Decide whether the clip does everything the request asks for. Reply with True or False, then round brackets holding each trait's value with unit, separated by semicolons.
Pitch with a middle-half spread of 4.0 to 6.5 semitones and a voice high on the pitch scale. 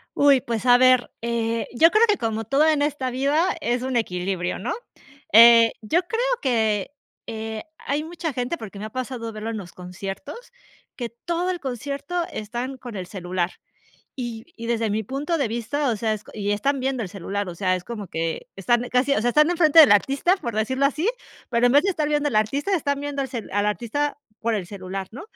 True (5.0 semitones; 240 Hz)